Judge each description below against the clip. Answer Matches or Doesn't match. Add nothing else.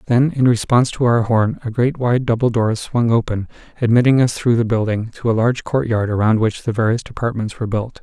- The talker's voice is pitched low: Matches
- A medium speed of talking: Doesn't match